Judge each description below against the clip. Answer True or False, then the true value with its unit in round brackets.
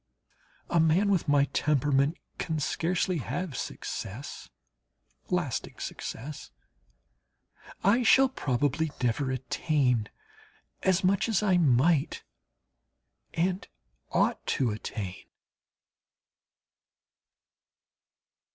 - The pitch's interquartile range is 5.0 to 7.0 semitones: True (5.6 semitones)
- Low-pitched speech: False (155 Hz)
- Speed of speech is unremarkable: False (80 wpm)